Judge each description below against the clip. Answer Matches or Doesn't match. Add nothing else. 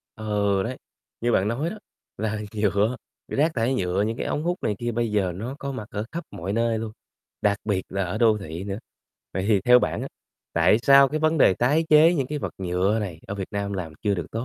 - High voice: Doesn't match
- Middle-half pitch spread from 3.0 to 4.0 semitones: Doesn't match